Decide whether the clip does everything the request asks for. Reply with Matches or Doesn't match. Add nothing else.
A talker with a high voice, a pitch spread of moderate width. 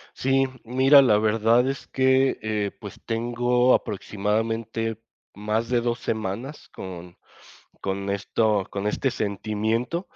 Doesn't match